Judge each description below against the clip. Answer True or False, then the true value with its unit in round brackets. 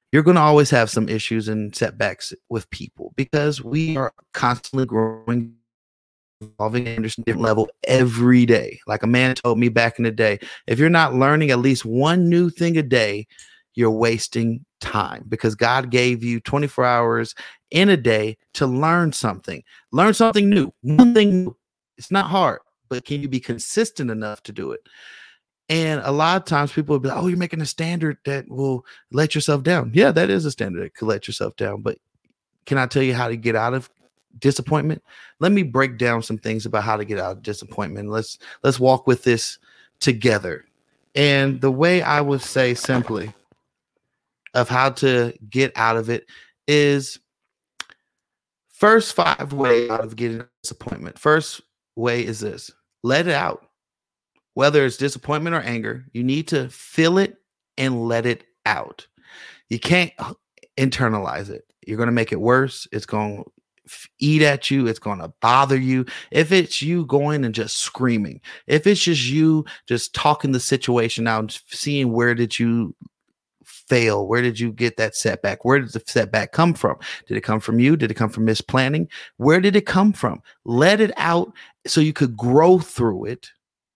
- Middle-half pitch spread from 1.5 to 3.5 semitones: False (4.7 semitones)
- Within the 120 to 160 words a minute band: False (185 wpm)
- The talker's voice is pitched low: True (130 Hz)